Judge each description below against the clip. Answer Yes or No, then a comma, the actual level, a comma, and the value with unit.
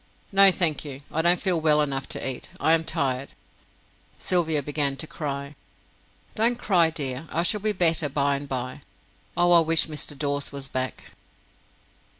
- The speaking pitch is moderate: Yes, medium, 150 Hz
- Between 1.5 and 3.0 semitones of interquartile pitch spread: No, average, 3.5 semitones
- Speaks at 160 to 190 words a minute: Yes, average, 165 wpm